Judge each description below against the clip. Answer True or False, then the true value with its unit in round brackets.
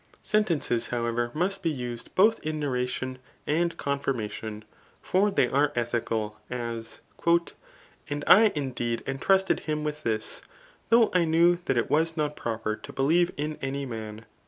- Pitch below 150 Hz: True (140 Hz)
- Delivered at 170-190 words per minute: True (175 wpm)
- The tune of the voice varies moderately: False (5.8 semitones)